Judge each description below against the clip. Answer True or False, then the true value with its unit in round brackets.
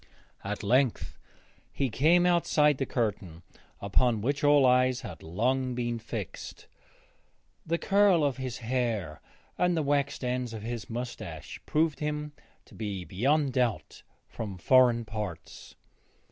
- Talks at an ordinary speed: False (130 wpm)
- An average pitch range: True (4.7 semitones)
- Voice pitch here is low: True (125 Hz)